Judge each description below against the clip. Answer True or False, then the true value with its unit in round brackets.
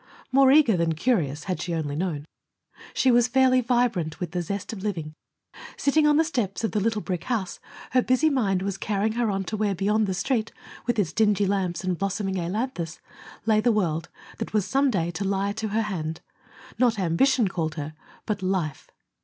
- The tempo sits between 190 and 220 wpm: True (195 wpm)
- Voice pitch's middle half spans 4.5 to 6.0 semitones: True (5.0 semitones)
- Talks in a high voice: True (200 Hz)